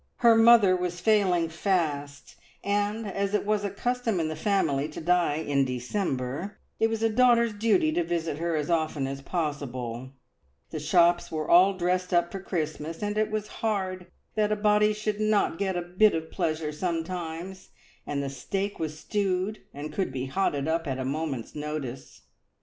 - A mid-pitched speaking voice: Yes, medium, 175 Hz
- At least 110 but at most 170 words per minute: No, average, 180 wpm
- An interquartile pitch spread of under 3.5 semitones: No, average, 5.2 semitones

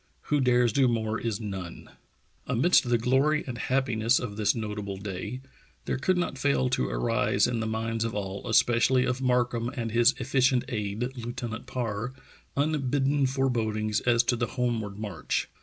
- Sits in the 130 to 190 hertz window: No, low, 120 Hz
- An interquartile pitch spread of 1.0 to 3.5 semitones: Yes, average, 2.8 semitones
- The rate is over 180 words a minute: No, average, 160 wpm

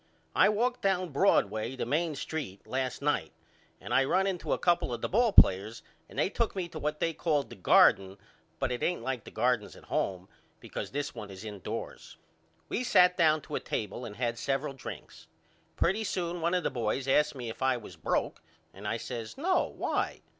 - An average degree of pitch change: No, wide, 7.7 semitones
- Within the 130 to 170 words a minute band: No, fast, 205 wpm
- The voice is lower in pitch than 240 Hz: Yes, low, 135 Hz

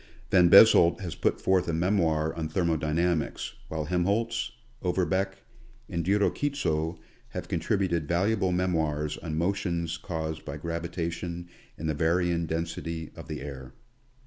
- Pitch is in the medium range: No, very low, 85 Hz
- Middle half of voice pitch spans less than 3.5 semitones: Yes, narrow, 2.4 semitones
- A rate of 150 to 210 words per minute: No, slow, 135 wpm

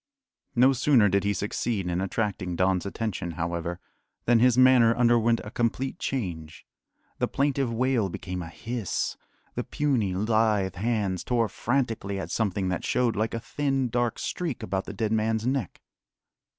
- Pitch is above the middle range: No, low, 110 Hz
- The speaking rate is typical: Yes, average, 155 wpm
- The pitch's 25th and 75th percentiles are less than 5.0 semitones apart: Yes, average, 4.3 semitones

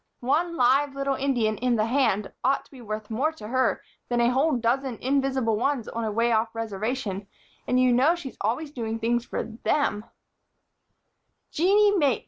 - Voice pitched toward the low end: No, high, 245 Hz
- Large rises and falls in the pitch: No, average, 3.6 semitones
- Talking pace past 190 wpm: No, average, 175 wpm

